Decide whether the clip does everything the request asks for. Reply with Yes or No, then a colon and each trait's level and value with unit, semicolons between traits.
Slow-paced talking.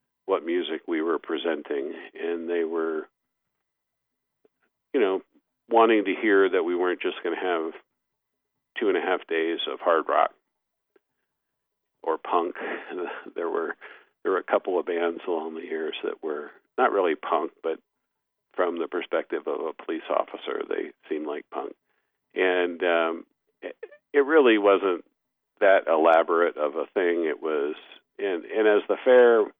No: average, 155 wpm